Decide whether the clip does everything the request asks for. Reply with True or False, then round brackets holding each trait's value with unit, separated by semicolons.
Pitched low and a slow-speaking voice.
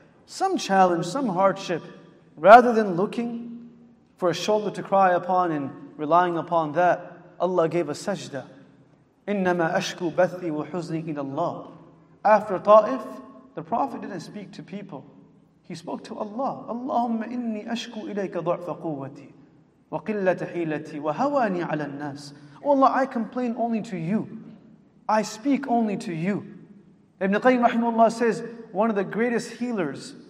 False (195 Hz; 130 wpm)